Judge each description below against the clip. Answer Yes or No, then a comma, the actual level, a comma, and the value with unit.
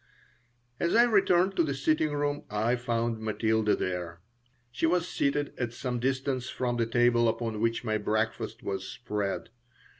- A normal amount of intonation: Yes, average, 4.4 semitones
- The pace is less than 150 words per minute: No, average, 155 wpm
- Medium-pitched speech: No, low, 120 Hz